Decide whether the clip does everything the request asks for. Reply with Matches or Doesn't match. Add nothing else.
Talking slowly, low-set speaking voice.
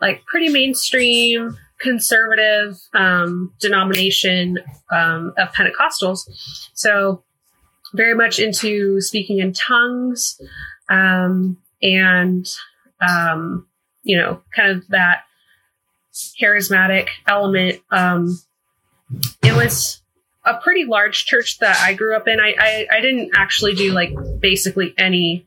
Doesn't match